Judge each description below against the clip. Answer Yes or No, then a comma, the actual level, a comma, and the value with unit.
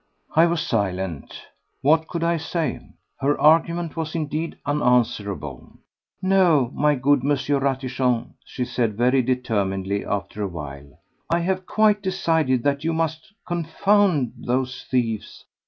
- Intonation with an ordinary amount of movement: No, wide, 5.7 semitones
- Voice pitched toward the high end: No, medium, 140 Hz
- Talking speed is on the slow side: Yes, slow, 130 wpm